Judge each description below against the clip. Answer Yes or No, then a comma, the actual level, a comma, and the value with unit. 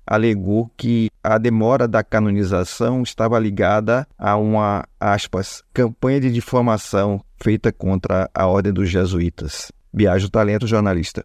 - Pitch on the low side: Yes, low, 105 Hz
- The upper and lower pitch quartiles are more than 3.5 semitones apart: No, average, 2.7 semitones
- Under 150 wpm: Yes, average, 125 wpm